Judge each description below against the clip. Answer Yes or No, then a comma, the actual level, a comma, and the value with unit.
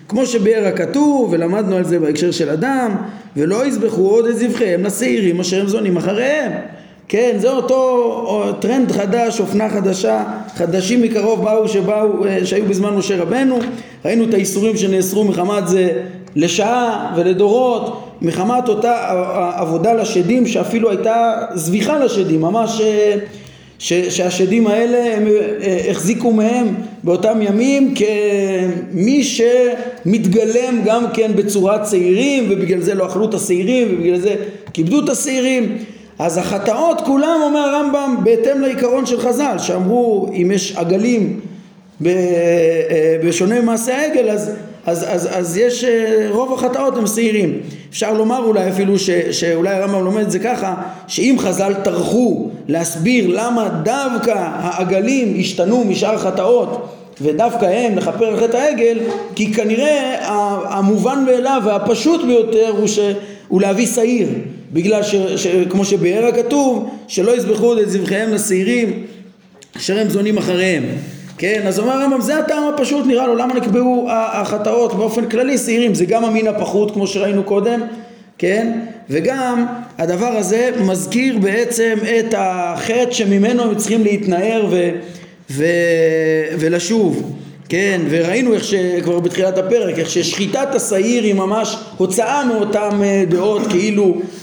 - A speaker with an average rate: Yes, average, 130 wpm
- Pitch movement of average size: Yes, average, 4.0 semitones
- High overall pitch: Yes, high, 210 Hz